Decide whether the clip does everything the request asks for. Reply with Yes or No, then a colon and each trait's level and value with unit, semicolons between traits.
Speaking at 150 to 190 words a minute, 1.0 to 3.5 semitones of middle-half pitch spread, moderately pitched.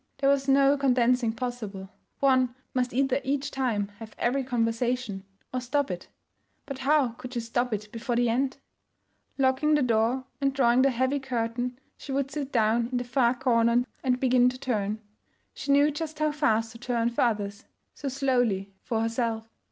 No: average, 175 wpm; average, 2.8 semitones; very high, 250 Hz